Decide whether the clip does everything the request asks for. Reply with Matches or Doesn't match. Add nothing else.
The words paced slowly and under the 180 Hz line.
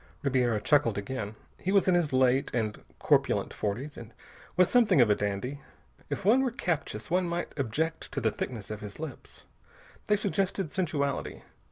Doesn't match